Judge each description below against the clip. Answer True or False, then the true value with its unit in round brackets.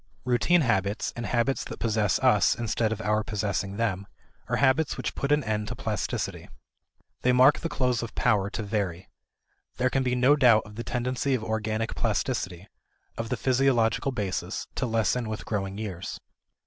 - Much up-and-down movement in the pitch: False (3.2 semitones)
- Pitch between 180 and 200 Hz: False (115 Hz)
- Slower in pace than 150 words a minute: False (175 wpm)